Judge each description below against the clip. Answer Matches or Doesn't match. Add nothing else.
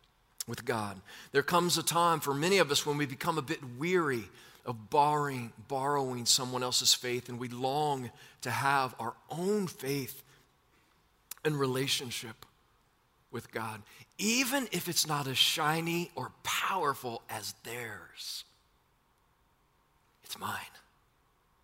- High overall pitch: Doesn't match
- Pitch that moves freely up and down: Doesn't match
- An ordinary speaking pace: Doesn't match